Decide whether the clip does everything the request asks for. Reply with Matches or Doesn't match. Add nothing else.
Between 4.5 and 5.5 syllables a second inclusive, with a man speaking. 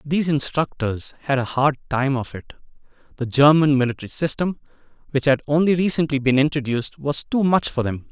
Doesn't match